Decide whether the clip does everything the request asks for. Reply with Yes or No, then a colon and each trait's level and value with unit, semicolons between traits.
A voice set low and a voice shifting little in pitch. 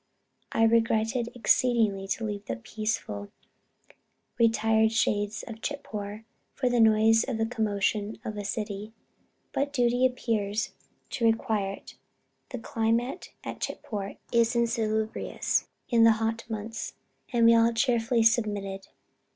No: high, 225 Hz; narrow, 1.6 semitones